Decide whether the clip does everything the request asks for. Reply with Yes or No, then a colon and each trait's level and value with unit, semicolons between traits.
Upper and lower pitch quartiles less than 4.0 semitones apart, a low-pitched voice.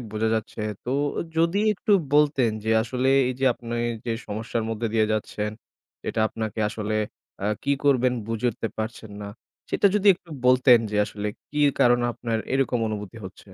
Yes: average, 2.9 semitones; low, 115 Hz